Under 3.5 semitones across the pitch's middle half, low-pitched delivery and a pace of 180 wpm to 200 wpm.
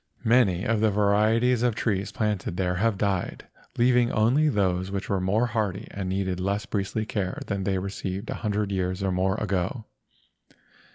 No: average, 2.7 semitones; low, 100 Hz; average, 170 wpm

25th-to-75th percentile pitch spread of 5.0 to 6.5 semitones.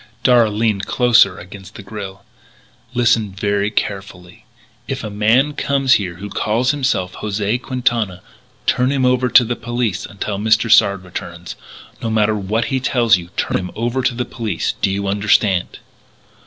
No: average, 3.6 semitones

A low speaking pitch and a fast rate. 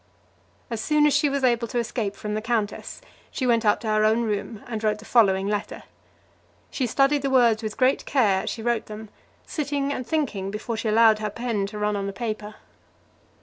No: high, 225 Hz; fast, 210 wpm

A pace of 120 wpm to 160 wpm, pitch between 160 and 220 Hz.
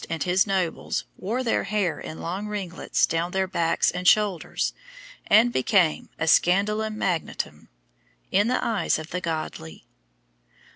Yes: average, 140 wpm; medium, 185 Hz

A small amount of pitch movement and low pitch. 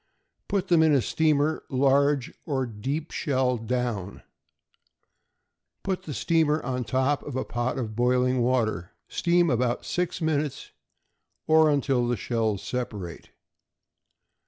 No: average, 4.0 semitones; low, 130 Hz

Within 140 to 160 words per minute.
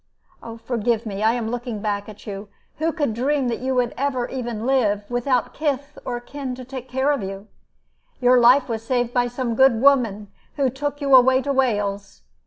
No: average, 190 wpm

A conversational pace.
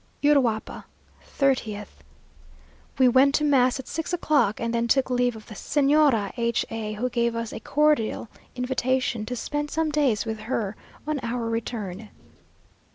Yes: average, 155 wpm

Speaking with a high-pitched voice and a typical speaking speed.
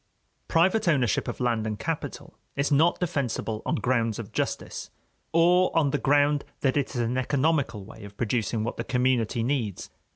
No: low, 130 Hz; average, 170 wpm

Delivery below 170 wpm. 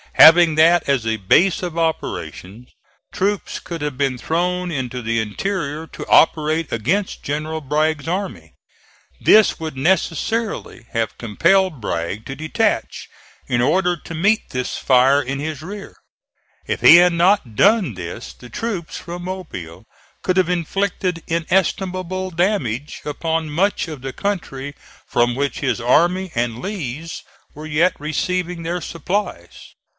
Yes: average, 140 wpm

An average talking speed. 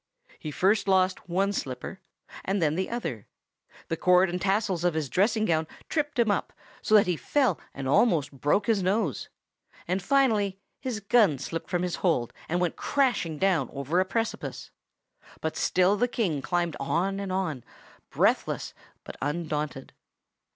Yes: average, 160 wpm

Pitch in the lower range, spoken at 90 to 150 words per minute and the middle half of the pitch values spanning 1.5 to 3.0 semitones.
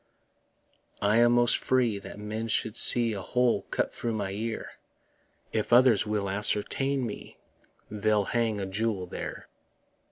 Yes: low, 110 Hz; average, 140 wpm; narrow, 2.4 semitones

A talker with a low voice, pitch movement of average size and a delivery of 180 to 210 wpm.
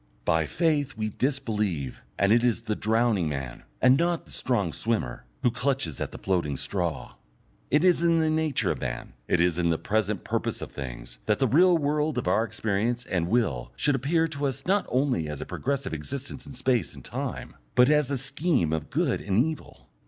No: low, 120 Hz; wide, 8.2 semitones; average, 200 wpm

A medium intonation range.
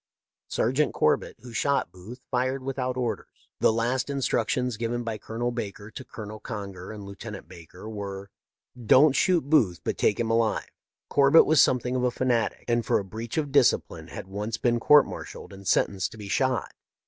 Yes: average, 3.8 semitones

